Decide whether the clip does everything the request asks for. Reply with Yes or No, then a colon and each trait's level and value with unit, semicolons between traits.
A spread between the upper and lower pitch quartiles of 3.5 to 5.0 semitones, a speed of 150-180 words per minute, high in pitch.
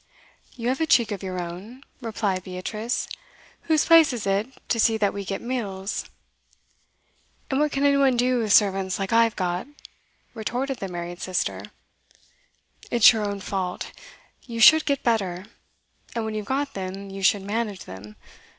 Yes: average, 4.3 semitones; average, 165 wpm; high, 215 Hz